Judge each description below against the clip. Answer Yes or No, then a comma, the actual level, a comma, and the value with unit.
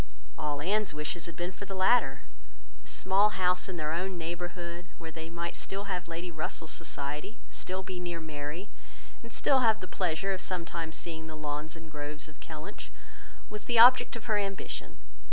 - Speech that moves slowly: No, average, 185 wpm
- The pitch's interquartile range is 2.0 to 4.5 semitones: Yes, average, 3.3 semitones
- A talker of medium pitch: Yes, medium, 175 Hz